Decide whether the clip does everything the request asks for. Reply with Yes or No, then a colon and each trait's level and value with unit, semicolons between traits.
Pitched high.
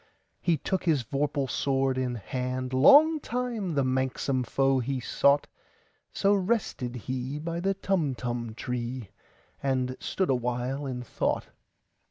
No: low, 135 Hz